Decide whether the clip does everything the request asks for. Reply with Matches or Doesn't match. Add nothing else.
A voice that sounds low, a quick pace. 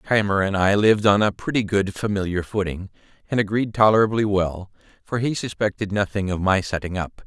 Doesn't match